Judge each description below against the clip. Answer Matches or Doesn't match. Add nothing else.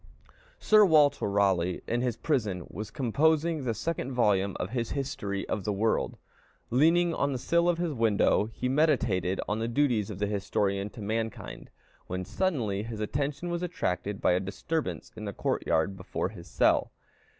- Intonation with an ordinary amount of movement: Doesn't match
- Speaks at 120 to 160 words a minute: Doesn't match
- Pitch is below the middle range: Matches